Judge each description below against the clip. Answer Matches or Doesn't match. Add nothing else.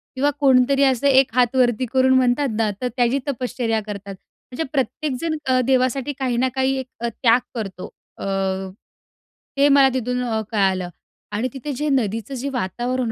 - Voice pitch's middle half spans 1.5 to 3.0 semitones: Matches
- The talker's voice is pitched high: Matches